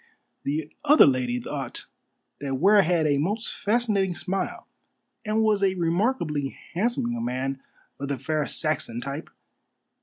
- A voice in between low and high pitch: Yes, medium, 160 Hz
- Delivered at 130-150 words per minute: Yes, average, 140 wpm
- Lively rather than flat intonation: Yes, wide, 6.6 semitones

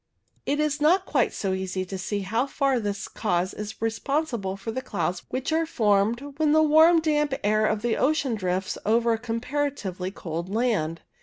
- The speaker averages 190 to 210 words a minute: No, average, 180 wpm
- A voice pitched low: No, high, 225 Hz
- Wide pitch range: Yes, wide, 6.6 semitones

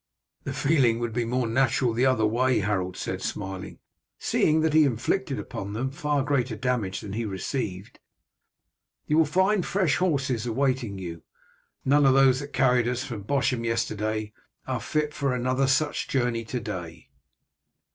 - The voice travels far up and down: No, average, 4.1 semitones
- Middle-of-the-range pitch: No, low, 125 Hz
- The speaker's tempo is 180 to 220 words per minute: No, average, 160 wpm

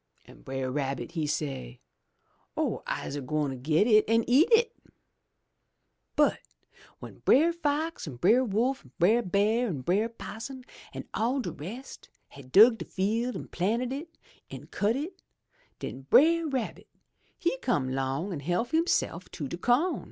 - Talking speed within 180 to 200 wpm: No, average, 155 wpm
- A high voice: Yes, high, 215 Hz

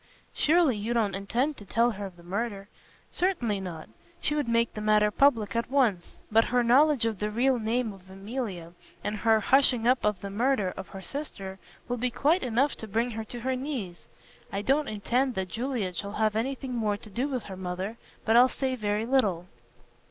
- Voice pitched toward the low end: No, high, 225 Hz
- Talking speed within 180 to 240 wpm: Yes, fast, 205 wpm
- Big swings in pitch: No, average, 4.2 semitones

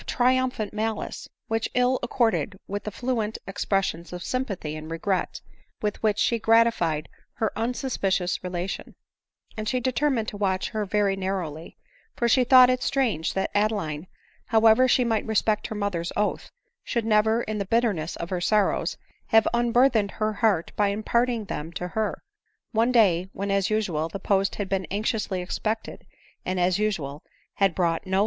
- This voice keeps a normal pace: Yes, average, 170 wpm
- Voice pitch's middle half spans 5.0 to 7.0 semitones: No, average, 3.4 semitones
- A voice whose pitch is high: Yes, high, 210 Hz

